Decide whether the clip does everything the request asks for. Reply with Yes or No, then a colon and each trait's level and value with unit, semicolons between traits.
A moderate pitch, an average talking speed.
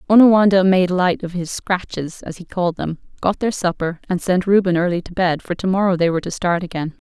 No: medium, 180 Hz; fast, 230 wpm